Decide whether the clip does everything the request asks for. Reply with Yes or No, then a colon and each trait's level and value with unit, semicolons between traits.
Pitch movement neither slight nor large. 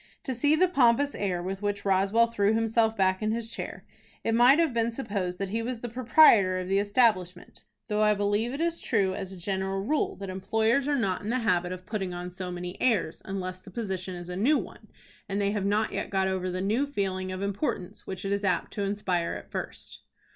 Yes: average, 3.5 semitones